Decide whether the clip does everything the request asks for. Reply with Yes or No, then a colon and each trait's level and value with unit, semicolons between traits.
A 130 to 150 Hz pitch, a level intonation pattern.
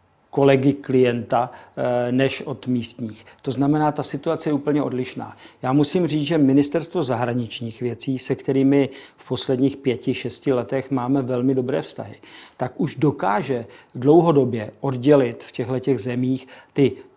Yes: low, 135 Hz; narrow, 2.2 semitones